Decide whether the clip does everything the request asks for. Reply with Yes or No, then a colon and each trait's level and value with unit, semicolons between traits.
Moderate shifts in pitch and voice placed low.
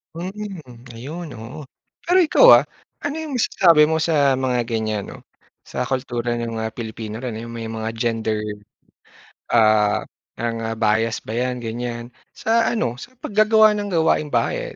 No: wide, 7.7 semitones; low, 120 Hz